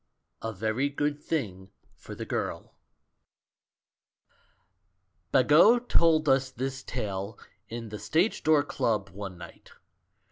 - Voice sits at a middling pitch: No, low, 130 Hz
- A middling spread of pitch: No, wide, 5.9 semitones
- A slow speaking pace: Yes, slow, 110 wpm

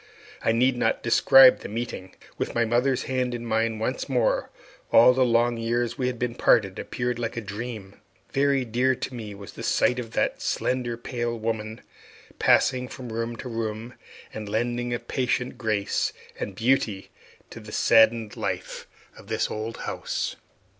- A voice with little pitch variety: Yes, narrow, 1.9 semitones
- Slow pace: No, average, 165 wpm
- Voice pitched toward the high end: No, low, 120 Hz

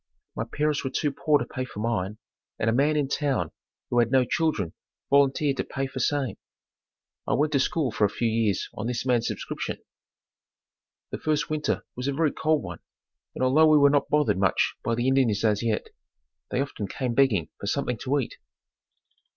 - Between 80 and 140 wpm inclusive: No, average, 195 wpm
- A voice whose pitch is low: Yes, low, 130 Hz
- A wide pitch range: No, average, 4.3 semitones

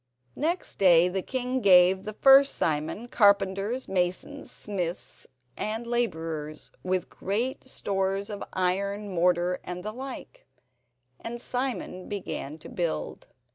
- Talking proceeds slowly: Yes, slow, 120 wpm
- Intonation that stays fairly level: No, average, 4.8 semitones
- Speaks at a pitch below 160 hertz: No, high, 195 Hz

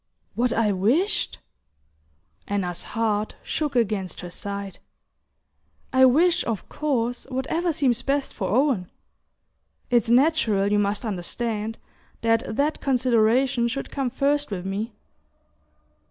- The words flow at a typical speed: No, slow, 115 wpm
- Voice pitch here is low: No, high, 235 Hz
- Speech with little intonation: No, average, 4.7 semitones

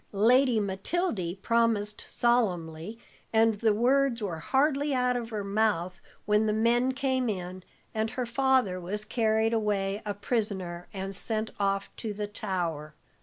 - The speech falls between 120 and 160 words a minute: Yes, average, 145 wpm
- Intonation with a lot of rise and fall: No, average, 3.6 semitones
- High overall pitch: Yes, high, 215 Hz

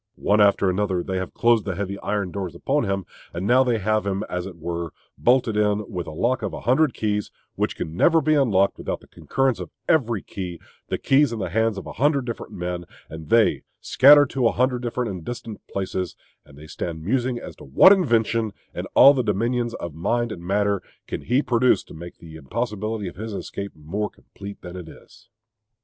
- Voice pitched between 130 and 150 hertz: No, low, 105 Hz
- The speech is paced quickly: Yes, fast, 210 wpm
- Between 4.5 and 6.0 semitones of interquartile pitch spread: Yes, average, 4.8 semitones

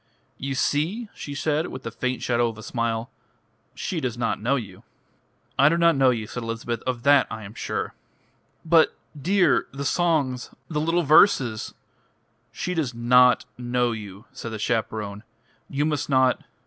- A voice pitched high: No, low, 125 Hz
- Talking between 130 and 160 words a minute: No, average, 170 wpm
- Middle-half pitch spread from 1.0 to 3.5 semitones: No, average, 4.5 semitones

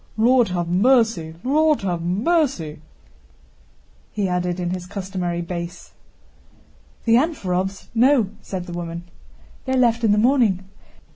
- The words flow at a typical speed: No, slow, 125 wpm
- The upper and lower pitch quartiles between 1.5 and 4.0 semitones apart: No, wide, 5.4 semitones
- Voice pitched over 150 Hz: Yes, high, 190 Hz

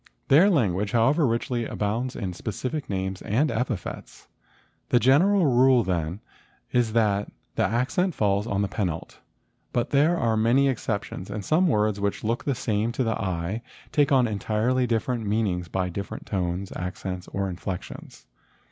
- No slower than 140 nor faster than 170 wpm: Yes, average, 155 wpm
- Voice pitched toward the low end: Yes, low, 110 Hz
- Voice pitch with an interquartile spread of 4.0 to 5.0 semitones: Yes, average, 4.6 semitones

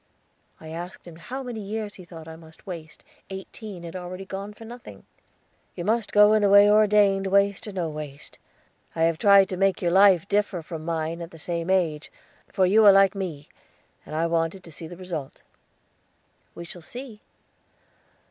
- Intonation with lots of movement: No, average, 3.5 semitones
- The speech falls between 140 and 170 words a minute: No, average, 185 wpm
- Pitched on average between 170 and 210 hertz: Yes, medium, 185 Hz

